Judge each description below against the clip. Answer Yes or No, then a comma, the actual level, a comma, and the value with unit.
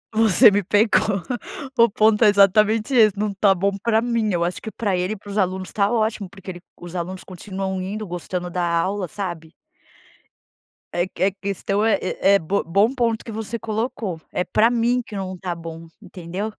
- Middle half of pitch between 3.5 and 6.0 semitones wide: No, average, 2.9 semitones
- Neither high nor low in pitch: No, high, 200 Hz